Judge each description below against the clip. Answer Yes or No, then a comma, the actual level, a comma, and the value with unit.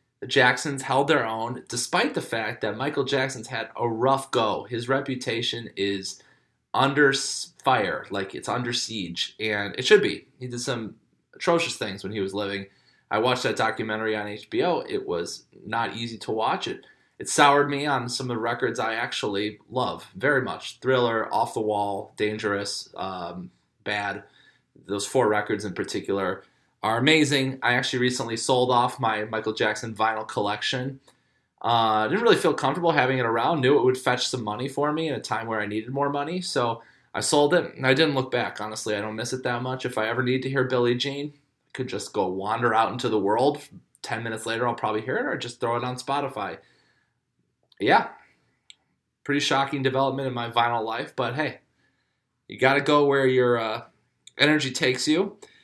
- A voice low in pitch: Yes, low, 120 Hz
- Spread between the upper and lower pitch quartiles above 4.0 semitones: No, average, 3.7 semitones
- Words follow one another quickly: No, average, 190 wpm